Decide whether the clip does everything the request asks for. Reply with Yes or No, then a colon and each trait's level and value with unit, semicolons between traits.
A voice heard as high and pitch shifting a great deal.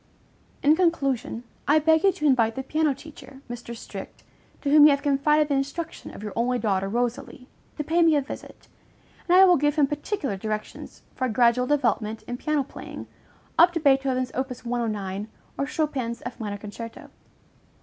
No: very high, 270 Hz; average, 4.3 semitones